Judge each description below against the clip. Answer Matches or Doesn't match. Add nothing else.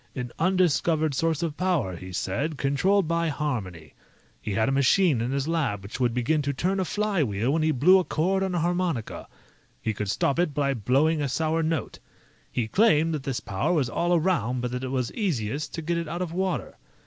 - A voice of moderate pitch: Matches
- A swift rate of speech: Matches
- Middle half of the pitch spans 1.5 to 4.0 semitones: Doesn't match